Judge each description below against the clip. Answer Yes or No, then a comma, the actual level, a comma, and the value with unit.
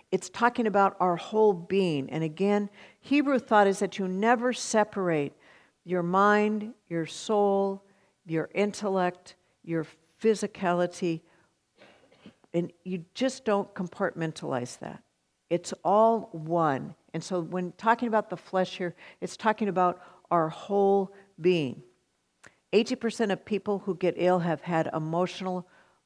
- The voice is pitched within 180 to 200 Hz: Yes, medium, 185 Hz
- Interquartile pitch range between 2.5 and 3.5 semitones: Yes, average, 3.1 semitones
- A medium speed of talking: No, slow, 125 wpm